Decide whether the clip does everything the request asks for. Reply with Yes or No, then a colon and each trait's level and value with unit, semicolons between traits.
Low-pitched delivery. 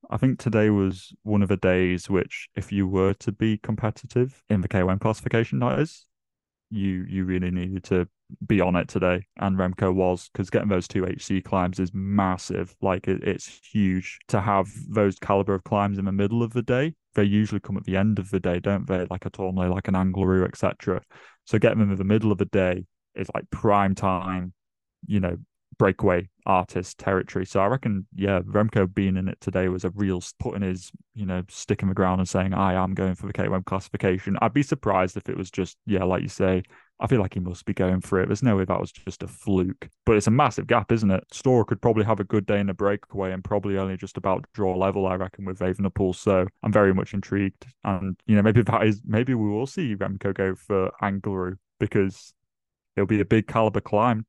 Yes: low, 100 Hz